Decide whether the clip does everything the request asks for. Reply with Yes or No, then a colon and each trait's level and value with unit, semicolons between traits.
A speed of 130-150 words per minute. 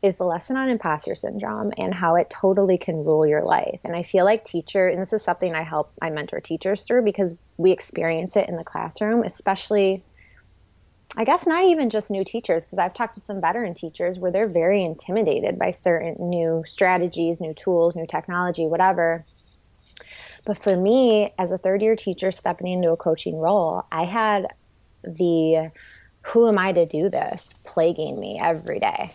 No: average, 185 wpm